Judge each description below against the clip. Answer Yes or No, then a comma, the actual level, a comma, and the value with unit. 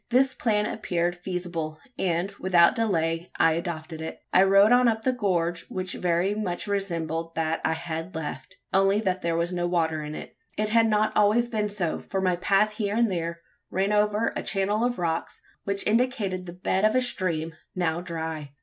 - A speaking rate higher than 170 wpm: Yes, average, 190 wpm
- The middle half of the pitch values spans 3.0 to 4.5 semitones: Yes, average, 3.9 semitones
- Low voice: No, medium, 185 Hz